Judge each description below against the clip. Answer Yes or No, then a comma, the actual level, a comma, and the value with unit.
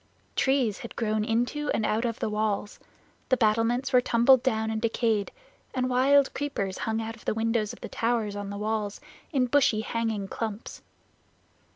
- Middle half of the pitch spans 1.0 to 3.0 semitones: Yes, narrow, 2.6 semitones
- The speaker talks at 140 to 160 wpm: No, average, 175 wpm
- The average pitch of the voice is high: Yes, high, 225 Hz